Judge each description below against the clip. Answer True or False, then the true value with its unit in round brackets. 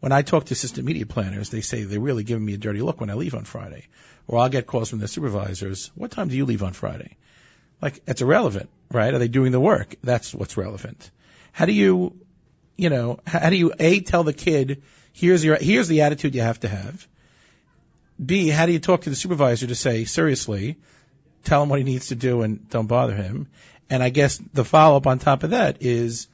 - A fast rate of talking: True (230 wpm)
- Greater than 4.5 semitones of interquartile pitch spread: True (5.1 semitones)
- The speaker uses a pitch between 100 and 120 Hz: False (130 Hz)